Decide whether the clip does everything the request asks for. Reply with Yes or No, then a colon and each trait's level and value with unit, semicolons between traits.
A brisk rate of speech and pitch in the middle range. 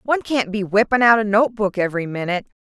No: fast, 230 wpm; high, 215 Hz